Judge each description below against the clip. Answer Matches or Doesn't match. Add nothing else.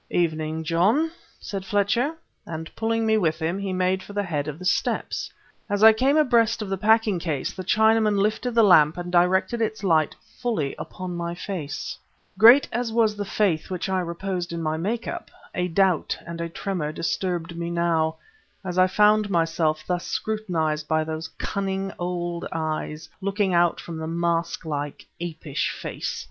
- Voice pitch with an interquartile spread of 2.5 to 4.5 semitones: Matches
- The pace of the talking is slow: Doesn't match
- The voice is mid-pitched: Matches